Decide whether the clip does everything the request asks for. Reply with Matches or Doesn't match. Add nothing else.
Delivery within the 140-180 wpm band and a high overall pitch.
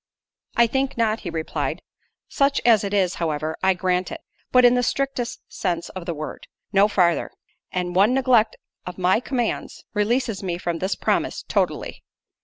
Matches